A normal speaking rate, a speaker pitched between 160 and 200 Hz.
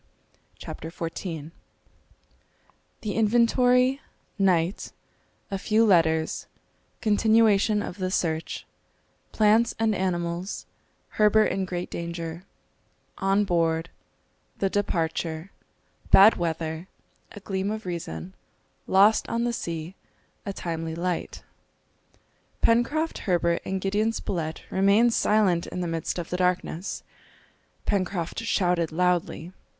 No: slow, 105 wpm; medium, 185 Hz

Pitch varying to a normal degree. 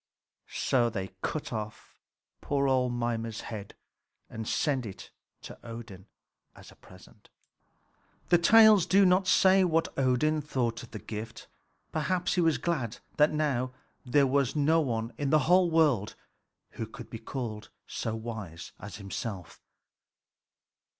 No: wide, 5.7 semitones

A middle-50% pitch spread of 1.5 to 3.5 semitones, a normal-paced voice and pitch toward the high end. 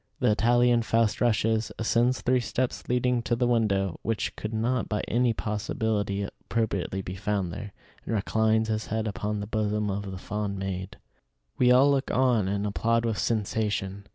No: narrow, 2.5 semitones; average, 170 wpm; low, 110 Hz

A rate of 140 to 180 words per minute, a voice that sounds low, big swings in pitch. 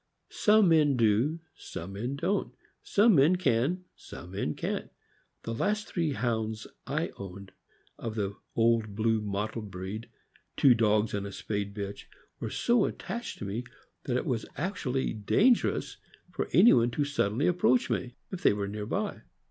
Yes: average, 160 wpm; low, 115 Hz; wide, 7.0 semitones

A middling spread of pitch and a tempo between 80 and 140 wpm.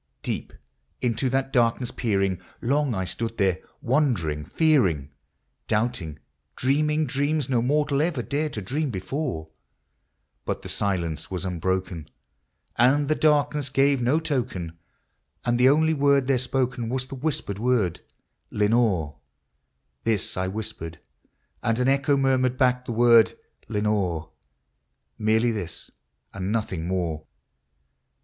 No: wide, 6.4 semitones; slow, 135 wpm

